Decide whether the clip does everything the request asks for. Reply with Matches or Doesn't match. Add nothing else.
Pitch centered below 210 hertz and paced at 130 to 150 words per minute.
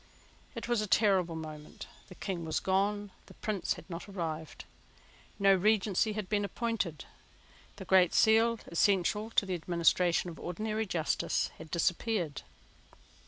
Matches